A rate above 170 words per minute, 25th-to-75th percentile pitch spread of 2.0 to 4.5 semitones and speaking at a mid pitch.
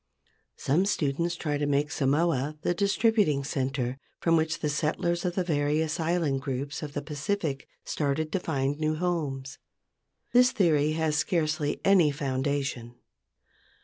No: average, 140 wpm; average, 3.3 semitones; medium, 150 Hz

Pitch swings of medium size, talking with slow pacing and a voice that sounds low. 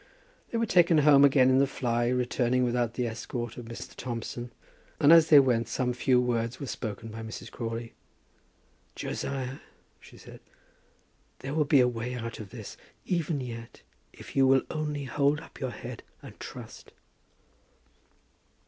No: average, 3.0 semitones; average, 160 wpm; low, 125 Hz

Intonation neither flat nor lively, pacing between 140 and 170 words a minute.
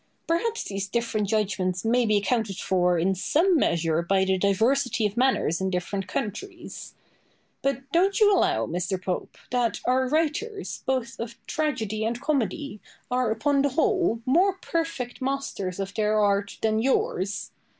No: wide, 6.2 semitones; average, 150 wpm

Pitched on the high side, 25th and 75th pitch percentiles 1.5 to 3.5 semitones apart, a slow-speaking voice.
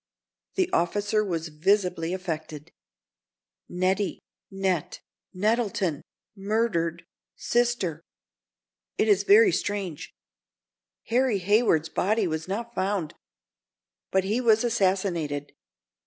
No: high, 195 Hz; average, 4.6 semitones; slow, 90 wpm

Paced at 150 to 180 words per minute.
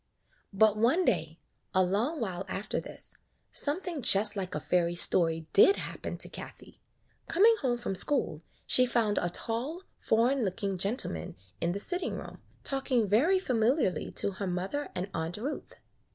Yes: average, 160 wpm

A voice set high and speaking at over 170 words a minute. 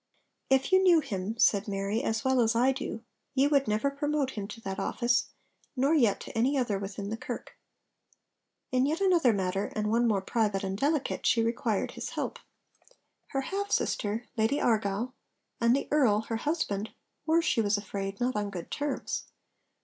Yes: high, 230 Hz; average, 180 wpm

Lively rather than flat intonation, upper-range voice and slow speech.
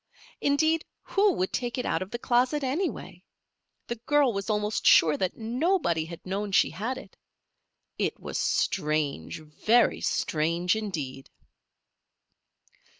Yes: wide, 7.4 semitones; high, 210 Hz; slow, 130 wpm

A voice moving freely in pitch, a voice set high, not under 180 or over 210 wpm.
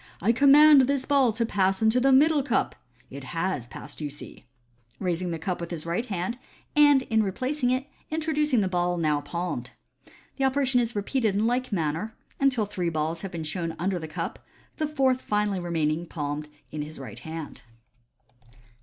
Yes: wide, 7.7 semitones; high, 195 Hz; average, 190 wpm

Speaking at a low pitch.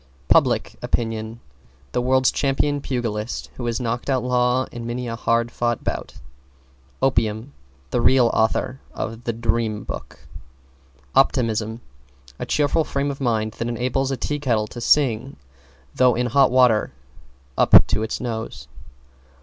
Yes: low, 120 Hz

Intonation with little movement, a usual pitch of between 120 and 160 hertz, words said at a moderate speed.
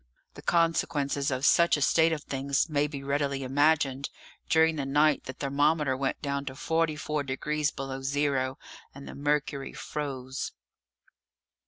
Yes: narrow, 1.8 semitones; medium, 140 Hz; average, 145 wpm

